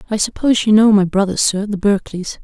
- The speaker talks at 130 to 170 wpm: No, fast, 220 wpm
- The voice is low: No, high, 205 Hz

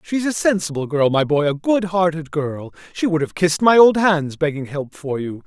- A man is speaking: Yes, male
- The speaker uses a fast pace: Yes, fast, 230 wpm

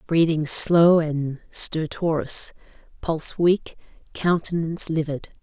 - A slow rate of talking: Yes, slow, 90 wpm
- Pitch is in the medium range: Yes, medium, 160 Hz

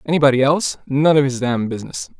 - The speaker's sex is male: Yes, male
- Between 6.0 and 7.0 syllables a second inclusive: Yes, 6.9 syllables/s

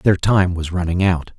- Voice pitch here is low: Yes, very low, 90 Hz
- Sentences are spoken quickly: Yes, fast, 215 wpm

